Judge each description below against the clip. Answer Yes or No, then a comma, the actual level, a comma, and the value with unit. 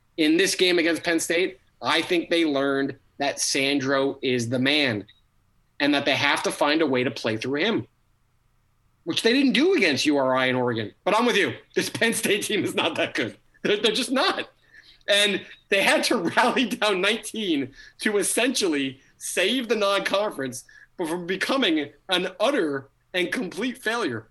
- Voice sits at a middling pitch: Yes, medium, 170 Hz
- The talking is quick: No, average, 175 wpm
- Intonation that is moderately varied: No, wide, 8.5 semitones